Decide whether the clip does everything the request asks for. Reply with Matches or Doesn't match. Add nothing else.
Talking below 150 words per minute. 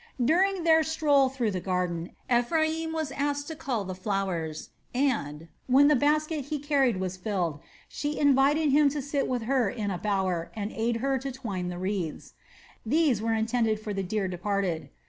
Doesn't match